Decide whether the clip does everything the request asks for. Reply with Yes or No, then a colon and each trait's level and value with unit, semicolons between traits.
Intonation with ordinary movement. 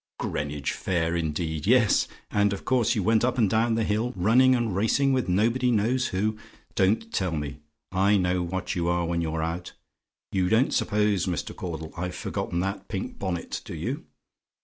Yes: average, 4.5 semitones